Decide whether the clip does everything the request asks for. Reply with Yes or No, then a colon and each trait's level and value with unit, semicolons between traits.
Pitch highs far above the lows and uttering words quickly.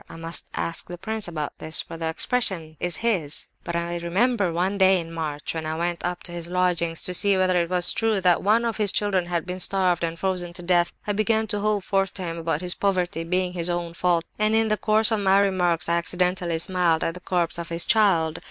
No: narrow, 2.5 semitones; fast, 240 wpm